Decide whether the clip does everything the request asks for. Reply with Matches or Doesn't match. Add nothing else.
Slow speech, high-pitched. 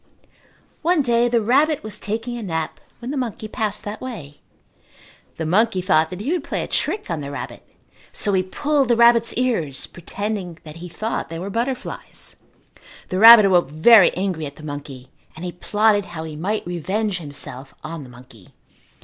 Doesn't match